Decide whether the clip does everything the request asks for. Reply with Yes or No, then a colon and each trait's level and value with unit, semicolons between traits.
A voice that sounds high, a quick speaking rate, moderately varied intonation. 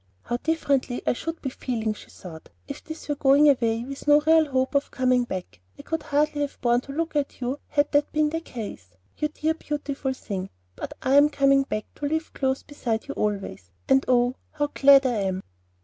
Yes: very high, 275 Hz; fast, 210 wpm; average, 3.5 semitones